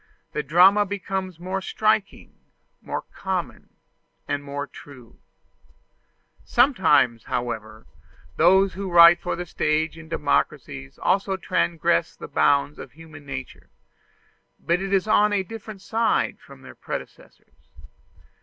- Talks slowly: Yes, slow, 120 wpm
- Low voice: No, medium, 175 Hz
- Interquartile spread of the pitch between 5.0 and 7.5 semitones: Yes, average, 5.3 semitones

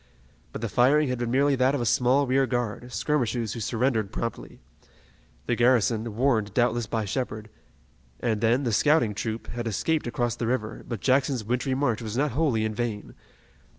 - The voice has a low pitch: Yes, low, 120 Hz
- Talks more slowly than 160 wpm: No, average, 180 wpm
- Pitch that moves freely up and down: No, average, 2.7 semitones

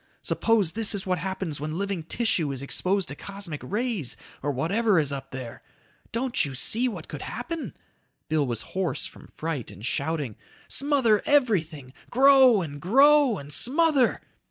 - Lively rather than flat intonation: Yes, wide, 8.3 semitones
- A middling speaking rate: Yes, average, 155 wpm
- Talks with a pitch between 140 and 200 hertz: Yes, high, 190 Hz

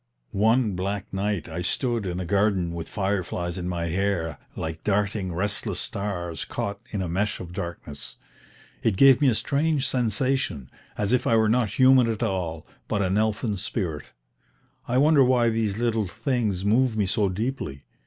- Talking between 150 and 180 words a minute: Yes, average, 170 wpm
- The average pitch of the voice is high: No, low, 100 Hz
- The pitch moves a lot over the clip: No, average, 4.3 semitones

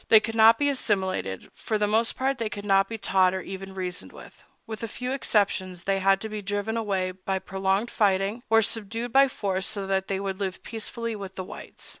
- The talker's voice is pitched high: Yes, high, 205 Hz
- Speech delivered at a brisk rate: Yes, fast, 220 wpm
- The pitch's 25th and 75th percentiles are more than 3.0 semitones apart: No, average, 2.7 semitones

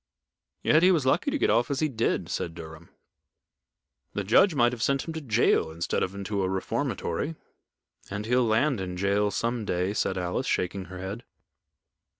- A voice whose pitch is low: Yes, low, 105 Hz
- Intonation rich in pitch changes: Yes, wide, 5.9 semitones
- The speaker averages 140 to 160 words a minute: No, average, 180 wpm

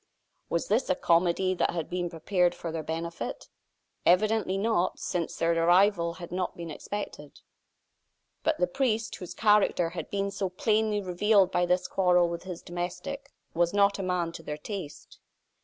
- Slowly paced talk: No, average, 165 wpm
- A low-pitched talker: No, medium, 180 Hz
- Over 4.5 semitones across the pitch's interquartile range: No, average, 2.8 semitones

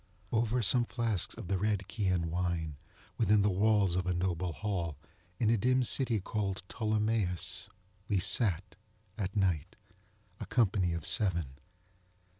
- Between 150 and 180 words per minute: No, average, 140 wpm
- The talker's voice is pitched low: Yes, low, 100 Hz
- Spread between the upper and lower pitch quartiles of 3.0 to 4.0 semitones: Yes, average, 3.4 semitones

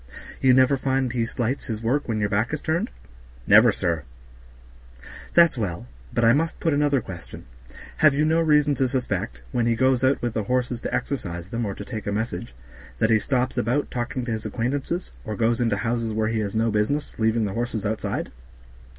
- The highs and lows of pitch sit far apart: No, average, 3.5 semitones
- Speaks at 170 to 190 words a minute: No, average, 200 wpm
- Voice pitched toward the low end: Yes, low, 120 Hz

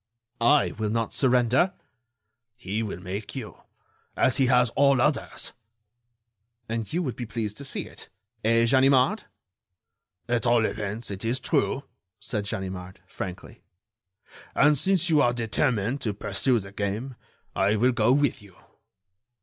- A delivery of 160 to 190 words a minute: No, average, 140 wpm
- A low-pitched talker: Yes, low, 115 Hz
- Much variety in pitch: No, average, 4.0 semitones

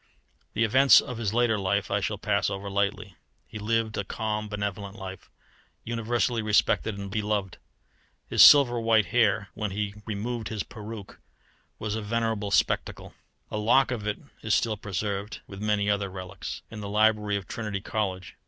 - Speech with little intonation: Yes, narrow, 1.8 semitones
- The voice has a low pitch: Yes, low, 105 Hz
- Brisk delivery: No, average, 165 wpm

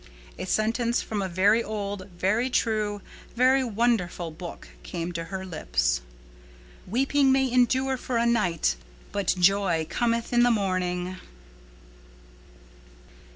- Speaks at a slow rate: Yes, slow, 120 wpm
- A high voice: Yes, high, 205 Hz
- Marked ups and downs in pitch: No, average, 4.9 semitones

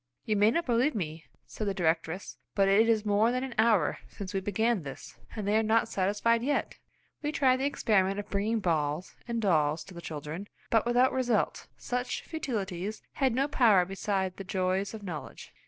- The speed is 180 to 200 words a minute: Yes, average, 190 wpm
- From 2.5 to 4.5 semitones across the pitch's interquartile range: Yes, average, 3.9 semitones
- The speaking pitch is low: No, high, 205 Hz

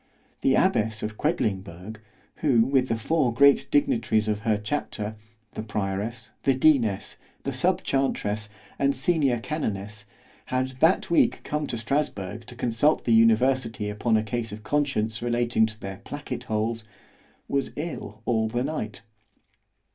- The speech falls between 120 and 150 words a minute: Yes, average, 140 wpm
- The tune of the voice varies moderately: Yes, average, 4.0 semitones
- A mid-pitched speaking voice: No, low, 115 Hz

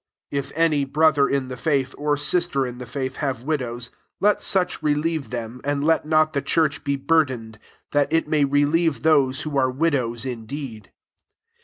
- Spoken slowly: No, average, 175 wpm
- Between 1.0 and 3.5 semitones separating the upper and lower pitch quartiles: Yes, average, 3.1 semitones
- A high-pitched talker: No, medium, 140 Hz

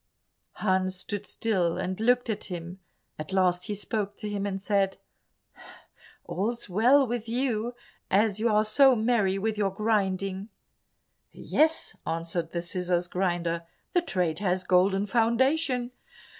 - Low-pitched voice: No, high, 200 Hz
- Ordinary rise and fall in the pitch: Yes, average, 3.6 semitones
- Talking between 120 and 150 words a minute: Yes, average, 140 wpm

